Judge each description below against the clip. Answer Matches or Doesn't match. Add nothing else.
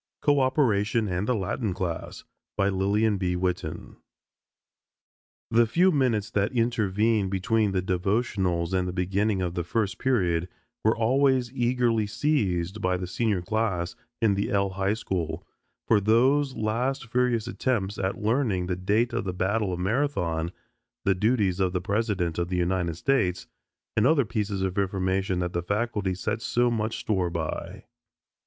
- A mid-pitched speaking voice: Doesn't match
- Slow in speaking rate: Doesn't match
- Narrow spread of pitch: Doesn't match